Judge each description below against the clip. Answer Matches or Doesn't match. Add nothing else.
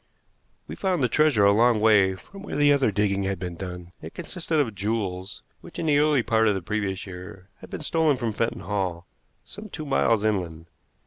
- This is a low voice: Matches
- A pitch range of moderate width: Doesn't match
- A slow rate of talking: Doesn't match